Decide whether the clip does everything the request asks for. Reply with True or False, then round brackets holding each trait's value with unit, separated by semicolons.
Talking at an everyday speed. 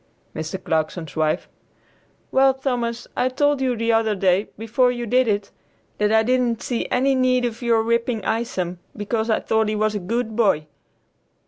True (175 wpm)